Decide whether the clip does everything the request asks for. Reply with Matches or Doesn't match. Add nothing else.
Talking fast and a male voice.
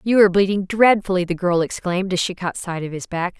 Doesn't match